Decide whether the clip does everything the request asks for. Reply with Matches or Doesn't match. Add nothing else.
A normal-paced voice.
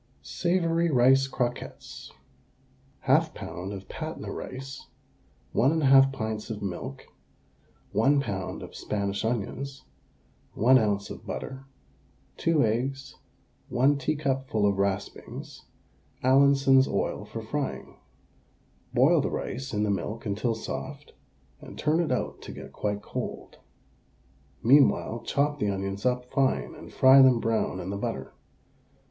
Doesn't match